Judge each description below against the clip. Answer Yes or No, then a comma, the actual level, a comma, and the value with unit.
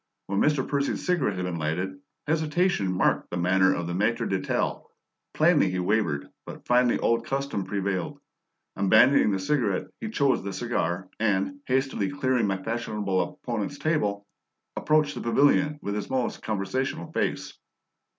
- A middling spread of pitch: No, wide, 6.5 semitones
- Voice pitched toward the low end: Yes, low, 105 Hz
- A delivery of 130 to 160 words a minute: Yes, average, 150 wpm